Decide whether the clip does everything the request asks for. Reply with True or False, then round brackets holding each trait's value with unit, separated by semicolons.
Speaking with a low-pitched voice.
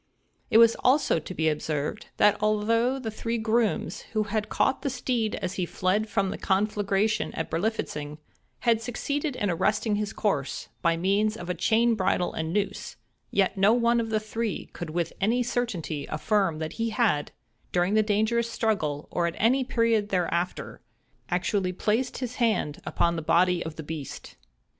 False (210 Hz)